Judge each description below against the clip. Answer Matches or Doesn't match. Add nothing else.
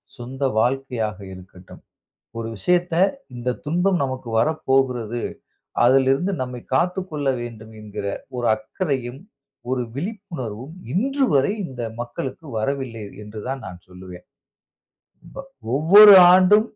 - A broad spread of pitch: Matches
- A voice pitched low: Matches